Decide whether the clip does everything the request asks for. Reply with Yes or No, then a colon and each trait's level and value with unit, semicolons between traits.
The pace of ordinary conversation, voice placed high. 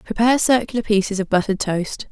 Yes: average, 170 wpm; high, 210 Hz